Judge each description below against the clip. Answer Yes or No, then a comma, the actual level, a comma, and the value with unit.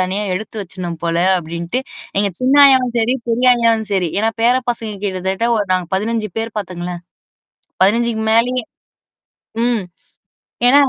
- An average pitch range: Yes, average, 4.2 semitones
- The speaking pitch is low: No, high, 220 Hz